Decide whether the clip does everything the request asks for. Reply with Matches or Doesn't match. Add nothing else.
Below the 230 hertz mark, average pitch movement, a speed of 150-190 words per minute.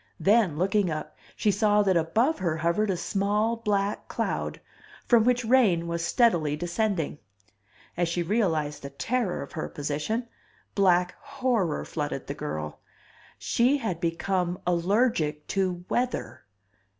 Doesn't match